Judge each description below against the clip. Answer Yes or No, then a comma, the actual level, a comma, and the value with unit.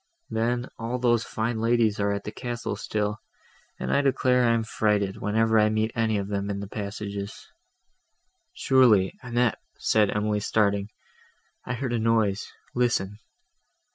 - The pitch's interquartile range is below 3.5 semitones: Yes, narrow, 2.5 semitones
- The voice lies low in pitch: Yes, low, 110 Hz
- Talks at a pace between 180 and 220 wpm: No, average, 150 wpm